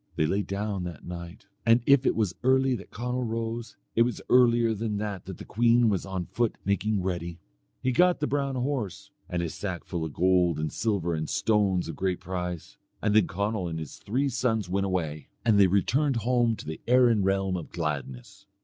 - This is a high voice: No, low, 100 Hz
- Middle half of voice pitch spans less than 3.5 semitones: No, average, 4.9 semitones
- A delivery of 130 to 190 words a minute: No, fast, 205 wpm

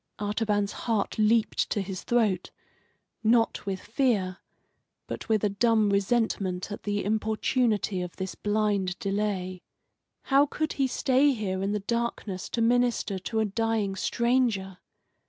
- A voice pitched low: No, high, 210 Hz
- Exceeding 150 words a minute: No, slow, 135 wpm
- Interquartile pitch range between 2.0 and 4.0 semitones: Yes, average, 3.1 semitones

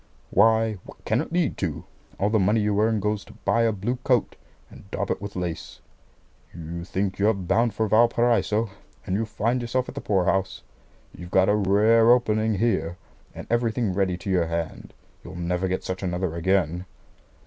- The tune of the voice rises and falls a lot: No, average, 3.4 semitones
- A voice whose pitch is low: Yes, low, 100 Hz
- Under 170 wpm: No, average, 185 wpm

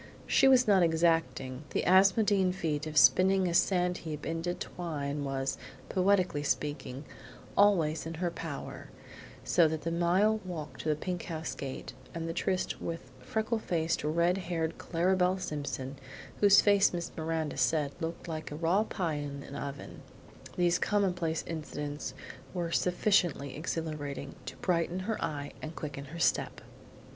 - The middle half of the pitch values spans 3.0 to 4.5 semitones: Yes, average, 3.5 semitones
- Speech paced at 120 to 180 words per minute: Yes, average, 150 wpm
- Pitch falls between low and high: Yes, medium, 165 Hz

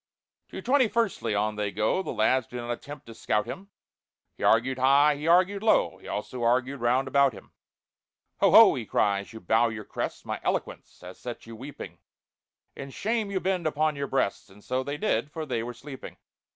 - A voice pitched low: Yes, low, 130 Hz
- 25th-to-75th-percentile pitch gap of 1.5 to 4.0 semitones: No, average, 5.1 semitones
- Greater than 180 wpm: Yes, average, 200 wpm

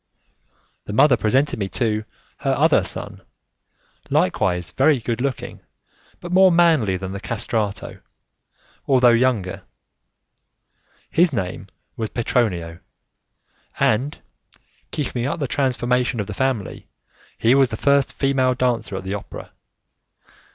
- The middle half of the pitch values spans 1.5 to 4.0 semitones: No, average, 4.7 semitones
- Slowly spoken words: Yes, slow, 120 wpm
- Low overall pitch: Yes, low, 120 Hz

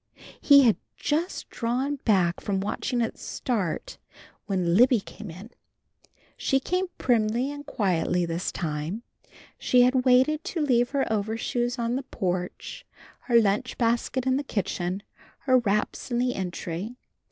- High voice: Yes, high, 235 Hz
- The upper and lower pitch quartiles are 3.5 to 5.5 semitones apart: Yes, average, 5.0 semitones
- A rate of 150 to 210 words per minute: No, average, 140 wpm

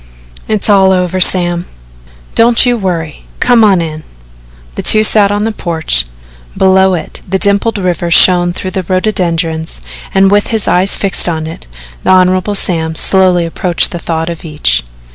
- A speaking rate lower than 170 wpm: Yes, average, 160 wpm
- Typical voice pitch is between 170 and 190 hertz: Yes, medium, 185 Hz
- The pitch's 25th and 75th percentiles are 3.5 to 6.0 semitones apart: No, average, 3.1 semitones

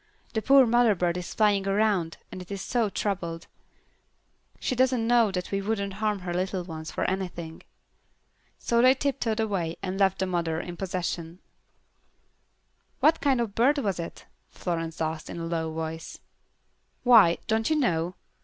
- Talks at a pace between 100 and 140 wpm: No, average, 160 wpm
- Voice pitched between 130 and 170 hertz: No, high, 195 Hz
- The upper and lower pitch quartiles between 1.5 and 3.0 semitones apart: No, average, 4.7 semitones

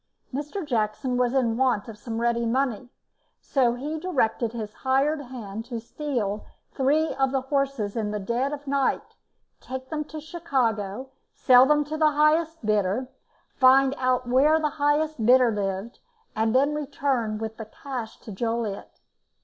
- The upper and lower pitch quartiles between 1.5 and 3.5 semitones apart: No, average, 4.2 semitones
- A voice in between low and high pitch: No, very high, 255 Hz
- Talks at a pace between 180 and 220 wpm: No, average, 155 wpm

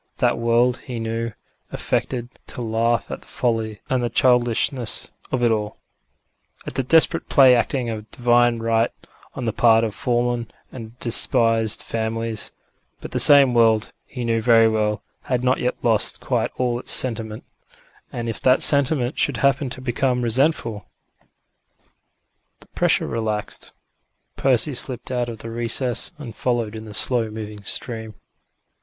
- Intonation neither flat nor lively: No, narrow, 1.9 semitones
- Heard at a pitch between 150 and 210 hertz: No, low, 120 Hz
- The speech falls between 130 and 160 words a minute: Yes, average, 150 wpm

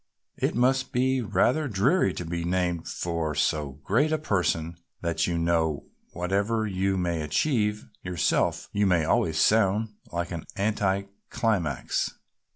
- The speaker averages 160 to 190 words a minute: No, average, 140 wpm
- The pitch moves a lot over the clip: No, average, 4.6 semitones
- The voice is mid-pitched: No, very low, 95 Hz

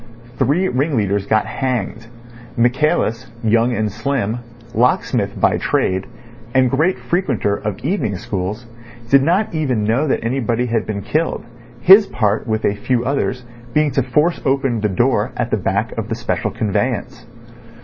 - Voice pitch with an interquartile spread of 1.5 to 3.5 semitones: No, average, 4.5 semitones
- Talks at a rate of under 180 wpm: Yes, average, 155 wpm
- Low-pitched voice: Yes, low, 125 Hz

